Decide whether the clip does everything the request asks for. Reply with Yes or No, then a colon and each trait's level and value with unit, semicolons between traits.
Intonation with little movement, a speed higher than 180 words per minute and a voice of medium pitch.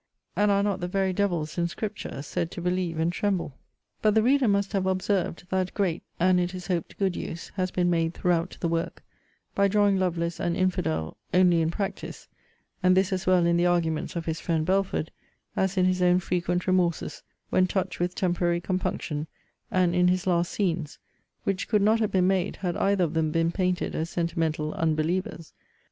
Yes: narrow, 2.0 semitones; average, 190 wpm; medium, 180 Hz